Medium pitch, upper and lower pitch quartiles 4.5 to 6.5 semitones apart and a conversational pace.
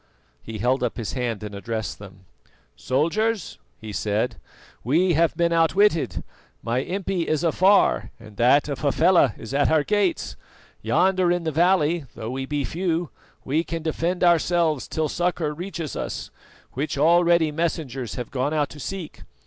Yes: medium, 155 Hz; average, 5.0 semitones; average, 155 wpm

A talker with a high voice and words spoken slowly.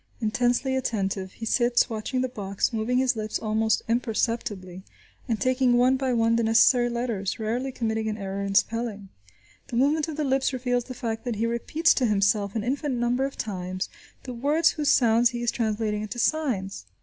No: high, 235 Hz; average, 185 wpm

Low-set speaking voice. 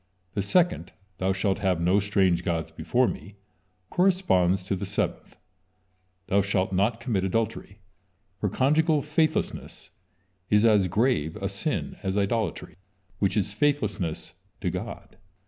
Yes: low, 100 Hz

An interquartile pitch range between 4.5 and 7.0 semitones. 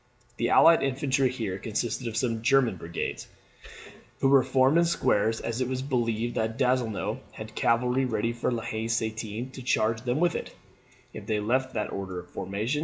No: average, 2.9 semitones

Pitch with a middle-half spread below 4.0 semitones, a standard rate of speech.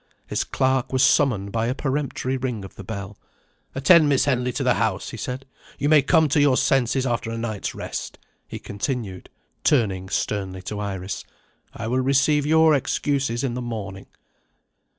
No: average, 4.8 semitones; average, 170 wpm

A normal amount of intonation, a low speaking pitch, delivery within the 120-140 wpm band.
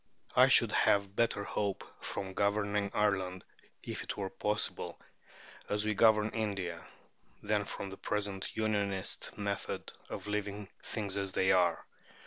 No: narrow, 1.4 semitones; low, 100 Hz; slow, 135 wpm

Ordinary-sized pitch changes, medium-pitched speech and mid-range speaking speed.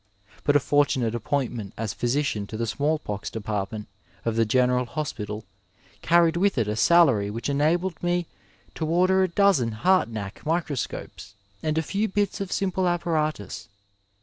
No: wide, 7.7 semitones; medium, 145 Hz; average, 150 wpm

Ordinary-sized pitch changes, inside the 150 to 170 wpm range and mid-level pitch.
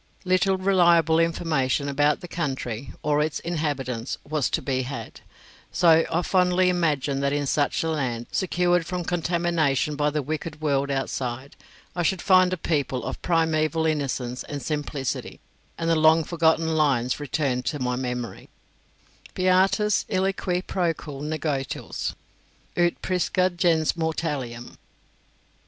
No: average, 3.9 semitones; slow, 135 wpm; medium, 155 Hz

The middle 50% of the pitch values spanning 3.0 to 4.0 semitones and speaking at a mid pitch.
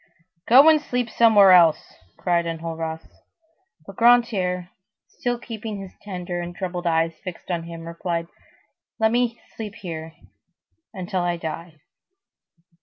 No: average, 4.7 semitones; medium, 180 Hz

